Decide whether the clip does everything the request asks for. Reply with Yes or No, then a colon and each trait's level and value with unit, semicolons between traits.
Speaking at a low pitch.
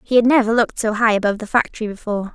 No: high, 220 Hz